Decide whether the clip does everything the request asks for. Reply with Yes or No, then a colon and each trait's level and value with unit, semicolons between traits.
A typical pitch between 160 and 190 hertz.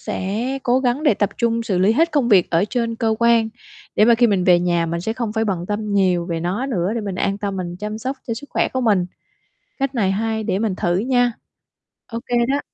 No: high, 215 Hz